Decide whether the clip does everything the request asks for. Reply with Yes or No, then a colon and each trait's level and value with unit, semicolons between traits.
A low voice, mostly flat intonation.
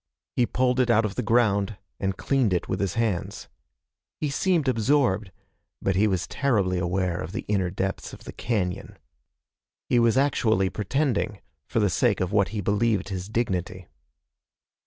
No: low, 105 Hz; average, 4.1 semitones